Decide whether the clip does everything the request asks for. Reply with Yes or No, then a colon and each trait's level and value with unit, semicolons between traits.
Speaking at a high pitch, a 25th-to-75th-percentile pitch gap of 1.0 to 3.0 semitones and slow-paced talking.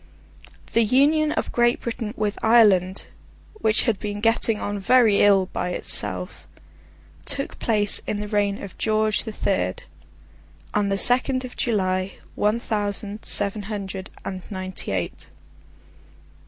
Yes: high, 210 Hz; narrow, 2.6 semitones; slow, 125 wpm